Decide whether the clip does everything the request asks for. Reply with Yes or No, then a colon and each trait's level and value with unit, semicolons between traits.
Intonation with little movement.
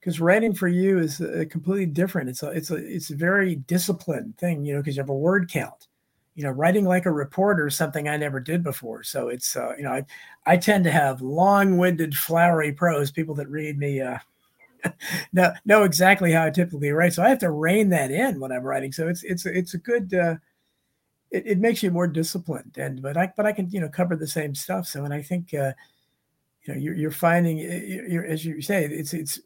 No: average, 3.4 semitones